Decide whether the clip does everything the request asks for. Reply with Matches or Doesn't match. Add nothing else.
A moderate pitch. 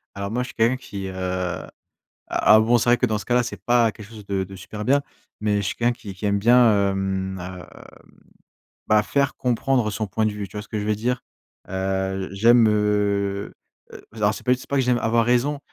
Doesn't match